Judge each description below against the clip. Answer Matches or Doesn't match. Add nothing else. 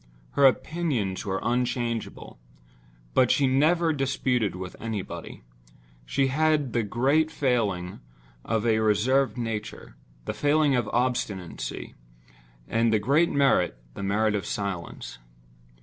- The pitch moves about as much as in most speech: Doesn't match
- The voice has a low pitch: Matches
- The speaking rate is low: Matches